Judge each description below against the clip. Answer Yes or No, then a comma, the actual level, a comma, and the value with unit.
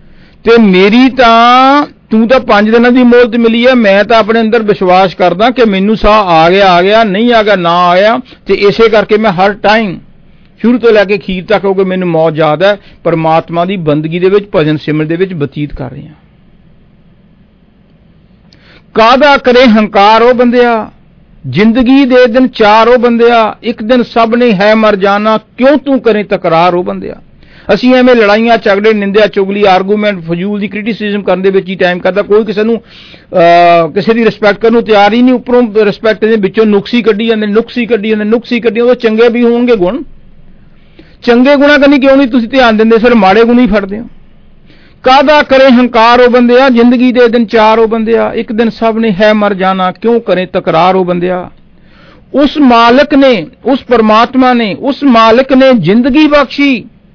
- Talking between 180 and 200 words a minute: Yes, average, 190 wpm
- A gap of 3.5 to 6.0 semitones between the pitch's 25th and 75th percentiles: Yes, average, 3.9 semitones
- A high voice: Yes, high, 220 Hz